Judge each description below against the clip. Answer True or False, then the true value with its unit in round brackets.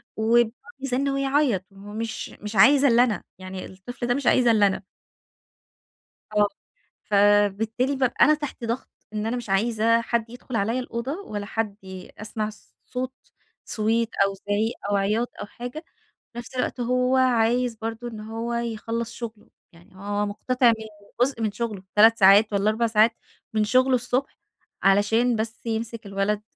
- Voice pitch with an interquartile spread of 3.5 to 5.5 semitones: False (2.9 semitones)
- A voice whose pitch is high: True (225 Hz)